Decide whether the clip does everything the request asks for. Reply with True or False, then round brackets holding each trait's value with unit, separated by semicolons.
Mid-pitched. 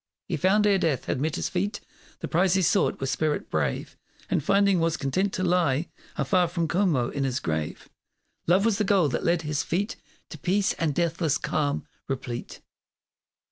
True (170 Hz)